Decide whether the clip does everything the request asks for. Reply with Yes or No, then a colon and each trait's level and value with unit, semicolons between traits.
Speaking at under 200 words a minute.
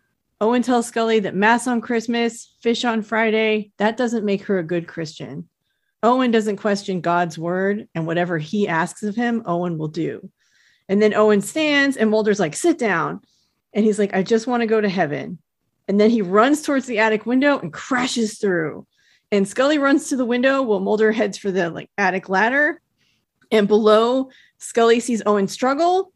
Yes: average, 185 wpm